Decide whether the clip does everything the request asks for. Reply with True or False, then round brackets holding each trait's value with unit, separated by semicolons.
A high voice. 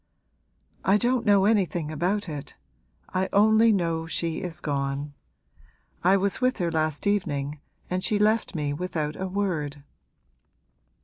False (180 Hz)